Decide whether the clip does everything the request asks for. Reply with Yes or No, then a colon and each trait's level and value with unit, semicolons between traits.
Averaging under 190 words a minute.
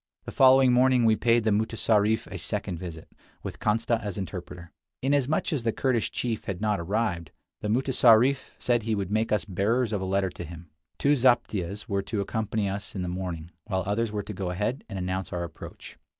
No: average, 200 wpm